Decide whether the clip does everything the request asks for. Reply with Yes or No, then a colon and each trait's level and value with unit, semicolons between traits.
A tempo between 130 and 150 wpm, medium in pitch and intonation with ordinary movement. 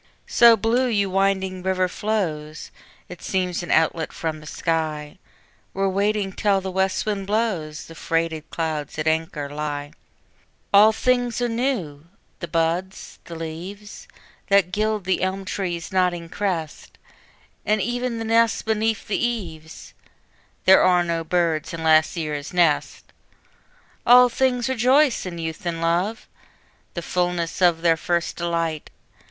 Yes: average, 140 wpm; medium, 180 Hz; average, 4.3 semitones